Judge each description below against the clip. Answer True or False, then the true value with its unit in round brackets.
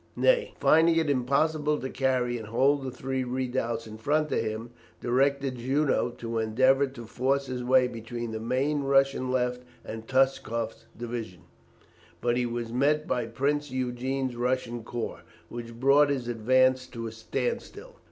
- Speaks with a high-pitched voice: False (130 Hz)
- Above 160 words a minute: False (155 wpm)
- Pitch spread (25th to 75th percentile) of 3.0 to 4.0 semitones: False (2.5 semitones)